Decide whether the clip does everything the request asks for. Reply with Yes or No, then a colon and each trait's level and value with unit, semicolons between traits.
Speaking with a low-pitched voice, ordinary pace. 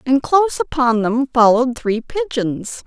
No: very high, 260 Hz; average, 145 wpm